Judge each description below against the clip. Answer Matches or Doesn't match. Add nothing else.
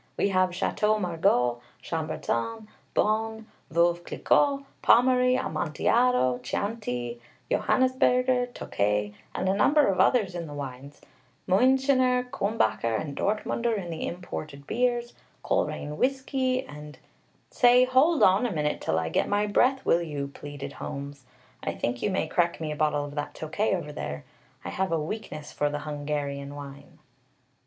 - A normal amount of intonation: Doesn't match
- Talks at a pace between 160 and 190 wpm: Doesn't match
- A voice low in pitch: Doesn't match